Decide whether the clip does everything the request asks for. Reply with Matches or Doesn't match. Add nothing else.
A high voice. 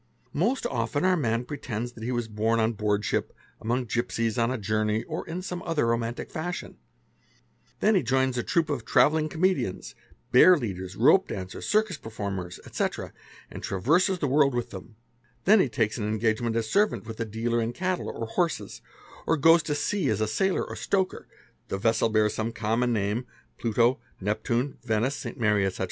Doesn't match